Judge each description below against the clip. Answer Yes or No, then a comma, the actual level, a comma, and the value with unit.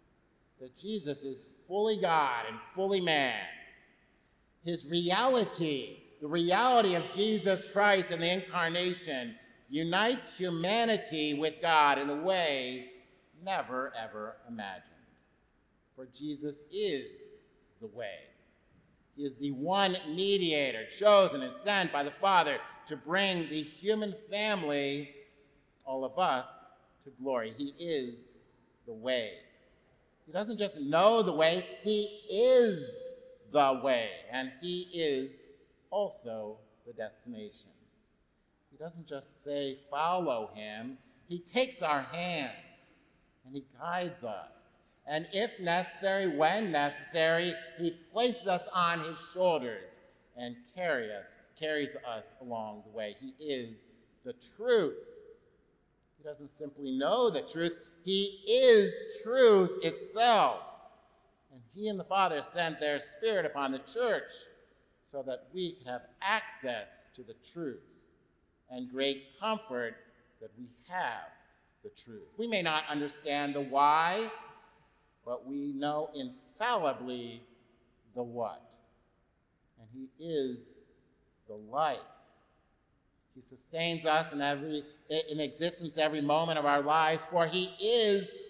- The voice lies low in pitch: No, medium, 165 Hz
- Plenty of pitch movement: Yes, wide, 6.6 semitones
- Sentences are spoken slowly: Yes, slow, 125 wpm